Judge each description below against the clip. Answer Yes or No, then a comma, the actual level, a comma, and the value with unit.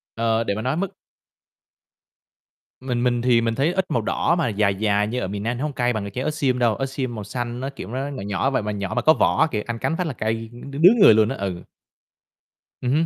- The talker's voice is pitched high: No, low, 120 Hz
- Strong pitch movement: No, average, 4.0 semitones